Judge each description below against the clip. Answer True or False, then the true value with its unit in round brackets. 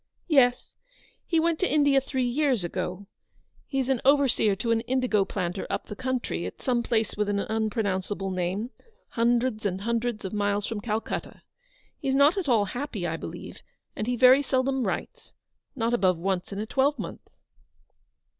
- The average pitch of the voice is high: True (230 Hz)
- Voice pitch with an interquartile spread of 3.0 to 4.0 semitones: False (4.5 semitones)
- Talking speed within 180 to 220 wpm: False (165 wpm)